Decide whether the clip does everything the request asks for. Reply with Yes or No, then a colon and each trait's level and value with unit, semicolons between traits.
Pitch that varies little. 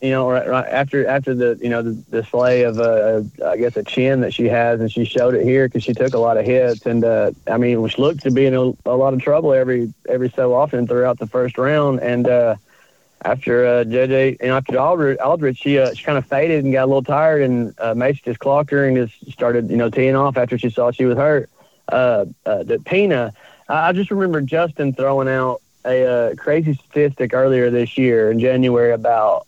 Yes: narrow, 2.1 semitones